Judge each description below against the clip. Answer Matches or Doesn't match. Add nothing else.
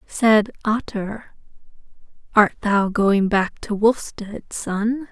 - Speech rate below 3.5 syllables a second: Matches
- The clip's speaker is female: Matches